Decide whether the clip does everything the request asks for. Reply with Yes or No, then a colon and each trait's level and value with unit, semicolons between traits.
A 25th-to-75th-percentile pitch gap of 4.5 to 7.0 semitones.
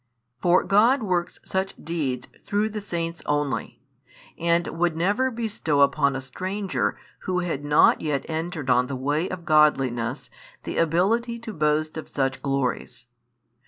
Yes: average, 5.1 semitones